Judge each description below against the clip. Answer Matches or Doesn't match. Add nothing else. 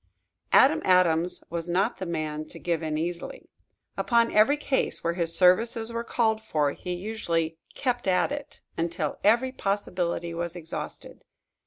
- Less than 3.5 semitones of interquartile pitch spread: Doesn't match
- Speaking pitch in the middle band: Matches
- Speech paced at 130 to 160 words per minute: Matches